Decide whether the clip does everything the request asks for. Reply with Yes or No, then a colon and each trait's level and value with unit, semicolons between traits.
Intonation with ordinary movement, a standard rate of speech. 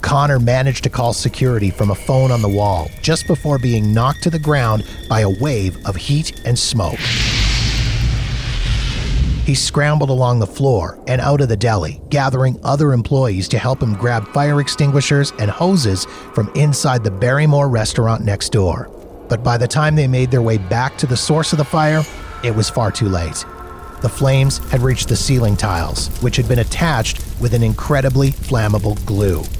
Yes: average, 4.4 semitones; average, 180 wpm